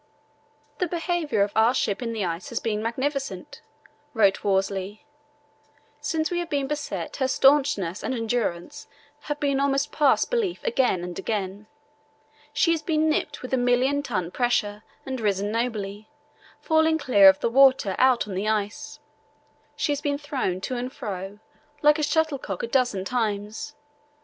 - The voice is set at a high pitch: Yes, high, 245 Hz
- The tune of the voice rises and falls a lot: Yes, wide, 6.1 semitones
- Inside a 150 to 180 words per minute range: Yes, average, 160 wpm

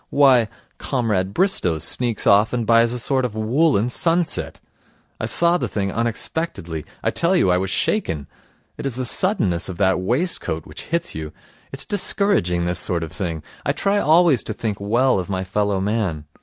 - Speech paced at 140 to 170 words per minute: No, average, 180 wpm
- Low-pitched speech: Yes, low, 110 Hz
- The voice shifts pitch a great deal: Yes, wide, 7.1 semitones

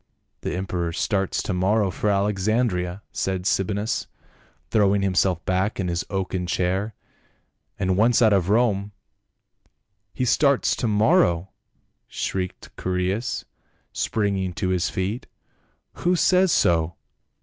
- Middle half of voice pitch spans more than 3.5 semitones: No, narrow, 2.6 semitones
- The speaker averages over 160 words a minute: No, average, 140 wpm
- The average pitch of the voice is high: No, very low, 95 Hz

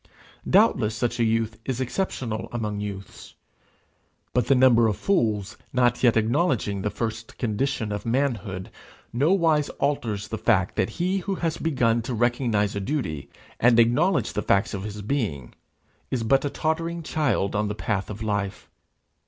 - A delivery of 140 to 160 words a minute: Yes, average, 155 wpm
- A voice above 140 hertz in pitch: No, low, 115 Hz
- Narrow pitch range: No, average, 4.6 semitones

